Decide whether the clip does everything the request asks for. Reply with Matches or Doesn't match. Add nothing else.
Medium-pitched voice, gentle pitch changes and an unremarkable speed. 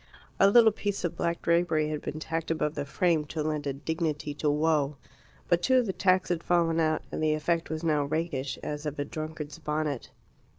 Doesn't match